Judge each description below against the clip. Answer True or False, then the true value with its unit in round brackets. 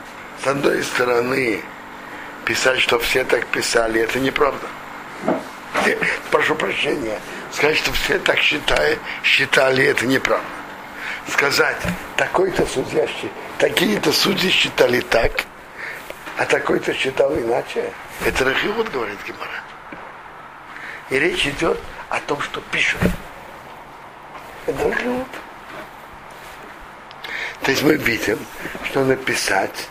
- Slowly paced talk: True (100 wpm)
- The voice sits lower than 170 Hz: True (135 Hz)